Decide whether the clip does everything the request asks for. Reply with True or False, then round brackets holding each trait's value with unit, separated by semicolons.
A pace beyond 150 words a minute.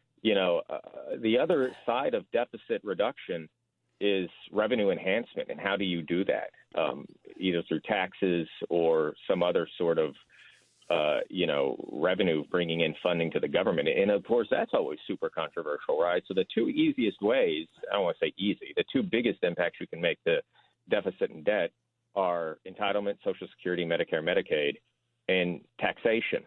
True (165 wpm)